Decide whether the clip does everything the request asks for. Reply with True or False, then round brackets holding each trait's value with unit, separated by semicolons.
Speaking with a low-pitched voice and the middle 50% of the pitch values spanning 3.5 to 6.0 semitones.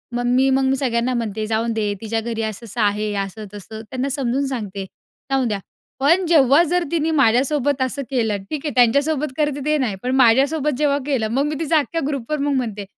False (260 Hz; 4.2 semitones)